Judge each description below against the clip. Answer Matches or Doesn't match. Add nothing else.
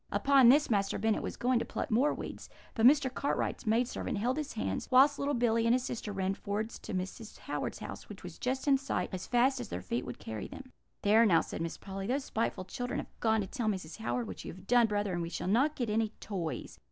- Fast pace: Matches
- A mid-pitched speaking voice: Doesn't match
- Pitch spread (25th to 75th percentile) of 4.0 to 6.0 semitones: Matches